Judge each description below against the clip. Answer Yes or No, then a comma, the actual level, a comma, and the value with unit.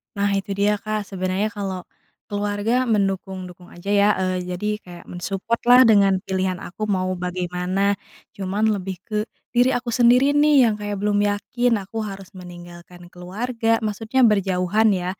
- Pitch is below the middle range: No, high, 200 Hz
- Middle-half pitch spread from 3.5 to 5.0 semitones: No, average, 2.8 semitones